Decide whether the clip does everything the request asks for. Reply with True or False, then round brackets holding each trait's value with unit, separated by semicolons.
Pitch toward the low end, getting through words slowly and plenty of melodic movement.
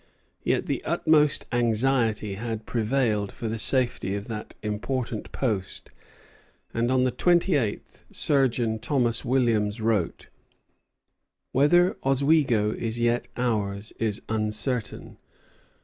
False (115 Hz; 110 wpm; 3.5 semitones)